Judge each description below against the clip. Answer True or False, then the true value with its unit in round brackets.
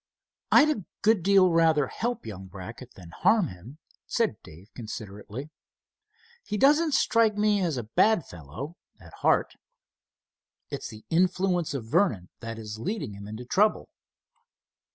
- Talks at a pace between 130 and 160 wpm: True (140 wpm)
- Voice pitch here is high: False (150 Hz)